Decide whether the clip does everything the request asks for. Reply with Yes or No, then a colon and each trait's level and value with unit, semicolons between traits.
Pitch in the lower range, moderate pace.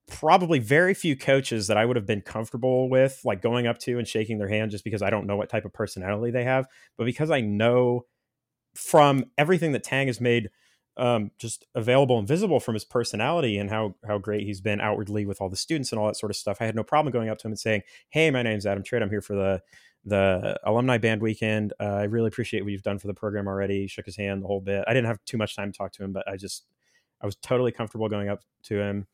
No: low, 110 Hz; fast, 260 wpm